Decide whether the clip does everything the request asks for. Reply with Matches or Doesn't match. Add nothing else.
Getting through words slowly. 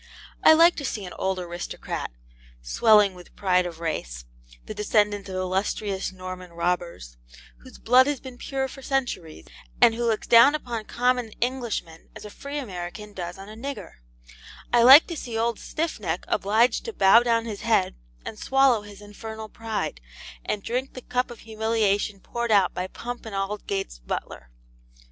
Doesn't match